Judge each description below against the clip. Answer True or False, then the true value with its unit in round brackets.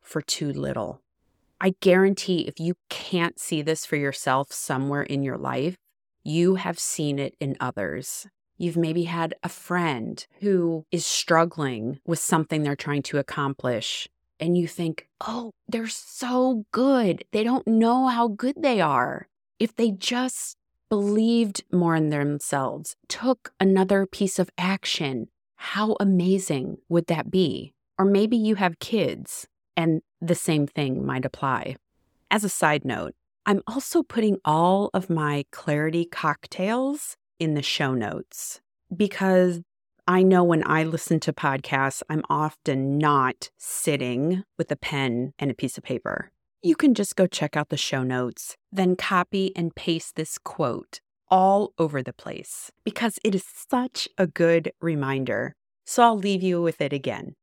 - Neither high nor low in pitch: True (170 Hz)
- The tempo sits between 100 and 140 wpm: False (155 wpm)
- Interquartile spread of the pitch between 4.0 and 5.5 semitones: True (5.1 semitones)